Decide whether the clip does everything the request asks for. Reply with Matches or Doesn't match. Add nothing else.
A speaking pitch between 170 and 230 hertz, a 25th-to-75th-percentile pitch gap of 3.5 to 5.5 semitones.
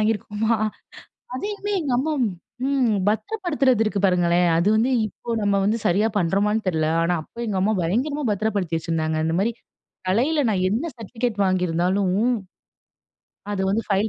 Matches